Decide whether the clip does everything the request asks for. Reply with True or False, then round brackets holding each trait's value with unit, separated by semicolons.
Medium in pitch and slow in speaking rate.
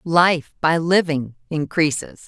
True (160 Hz; 105 wpm)